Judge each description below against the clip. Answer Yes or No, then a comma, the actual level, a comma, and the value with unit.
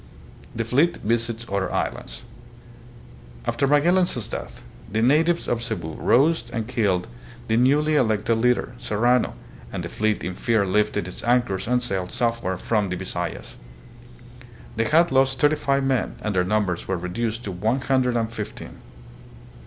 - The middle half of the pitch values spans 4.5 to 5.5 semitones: No, average, 4.1 semitones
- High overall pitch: No, low, 115 Hz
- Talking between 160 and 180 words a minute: Yes, average, 165 wpm